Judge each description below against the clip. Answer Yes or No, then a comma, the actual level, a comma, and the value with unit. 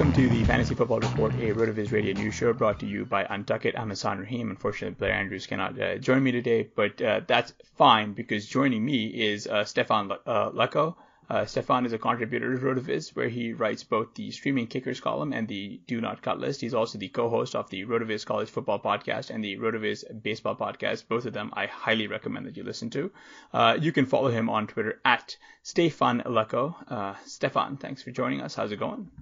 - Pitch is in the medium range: No, low, 115 Hz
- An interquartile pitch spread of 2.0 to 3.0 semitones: Yes, average, 2.7 semitones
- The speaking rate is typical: No, fast, 215 wpm